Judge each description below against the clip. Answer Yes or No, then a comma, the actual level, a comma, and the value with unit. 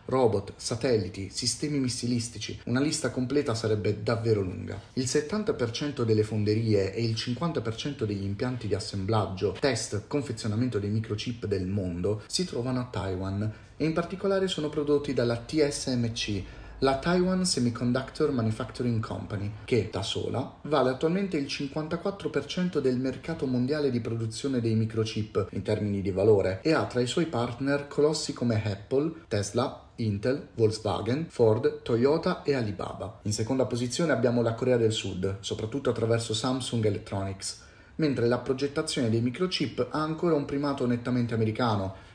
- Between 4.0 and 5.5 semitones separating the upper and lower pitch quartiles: Yes, average, 4.8 semitones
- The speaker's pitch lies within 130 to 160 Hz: No, low, 120 Hz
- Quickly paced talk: No, average, 140 wpm